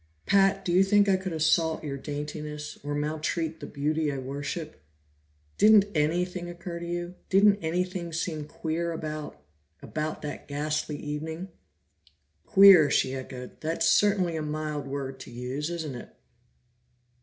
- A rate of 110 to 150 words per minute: Yes, average, 145 wpm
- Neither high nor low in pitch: Yes, medium, 155 Hz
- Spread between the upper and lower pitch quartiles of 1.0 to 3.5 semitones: Yes, average, 2.9 semitones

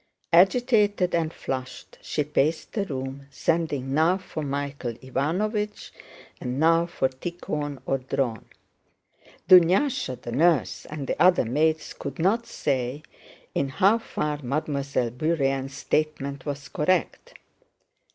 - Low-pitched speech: No, medium, 150 Hz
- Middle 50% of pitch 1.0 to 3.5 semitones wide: No, average, 4.1 semitones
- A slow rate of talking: Yes, slow, 120 wpm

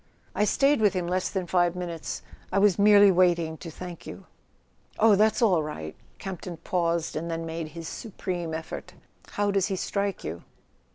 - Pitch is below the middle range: No, medium, 180 Hz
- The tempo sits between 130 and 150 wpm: No, average, 175 wpm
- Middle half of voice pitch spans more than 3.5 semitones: No, average, 3.2 semitones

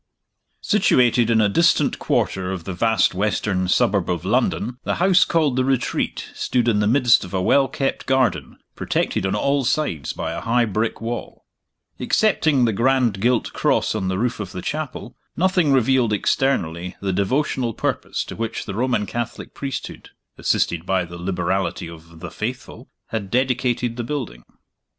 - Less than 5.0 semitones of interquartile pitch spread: No, wide, 5.5 semitones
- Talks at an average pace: Yes, average, 165 wpm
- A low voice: Yes, low, 115 Hz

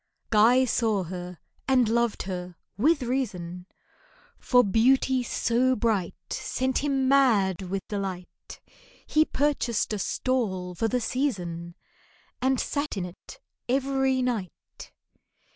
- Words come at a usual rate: No, slow, 115 wpm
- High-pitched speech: Yes, high, 230 Hz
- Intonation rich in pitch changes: Yes, wide, 5.7 semitones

